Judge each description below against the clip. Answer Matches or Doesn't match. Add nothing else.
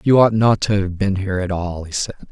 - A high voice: Doesn't match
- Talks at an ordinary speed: Doesn't match